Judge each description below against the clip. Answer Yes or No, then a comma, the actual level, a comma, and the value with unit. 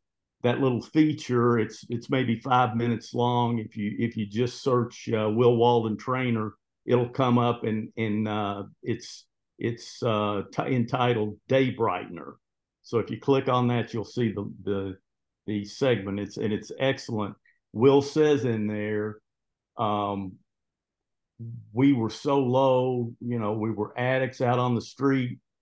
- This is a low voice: Yes, low, 115 Hz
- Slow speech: No, average, 155 wpm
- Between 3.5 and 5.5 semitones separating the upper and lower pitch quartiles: No, average, 2.9 semitones